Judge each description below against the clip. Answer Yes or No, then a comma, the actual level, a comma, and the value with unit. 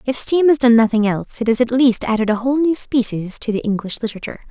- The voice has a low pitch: No, high, 235 Hz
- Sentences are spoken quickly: Yes, fast, 240 wpm